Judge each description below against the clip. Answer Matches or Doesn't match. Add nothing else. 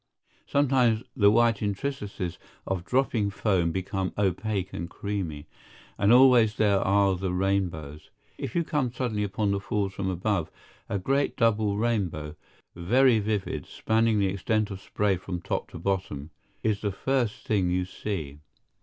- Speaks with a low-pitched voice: Matches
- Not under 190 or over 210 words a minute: Doesn't match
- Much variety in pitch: Doesn't match